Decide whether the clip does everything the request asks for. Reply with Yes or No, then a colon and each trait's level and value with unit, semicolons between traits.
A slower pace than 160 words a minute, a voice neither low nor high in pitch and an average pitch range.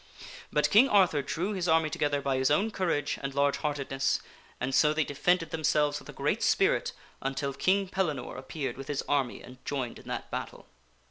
No: average, 190 wpm; medium, 145 Hz; average, 3.3 semitones